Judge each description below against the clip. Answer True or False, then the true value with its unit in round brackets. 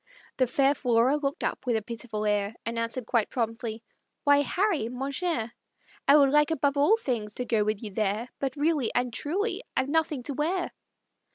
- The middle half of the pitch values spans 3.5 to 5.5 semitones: True (4.3 semitones)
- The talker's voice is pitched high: True (255 Hz)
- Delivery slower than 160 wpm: False (190 wpm)